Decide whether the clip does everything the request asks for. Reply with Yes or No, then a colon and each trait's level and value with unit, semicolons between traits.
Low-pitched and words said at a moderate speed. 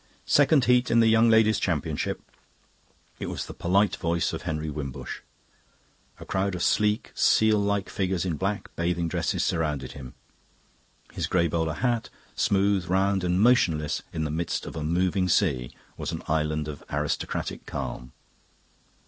Yes: very low, 90 Hz; average, 155 wpm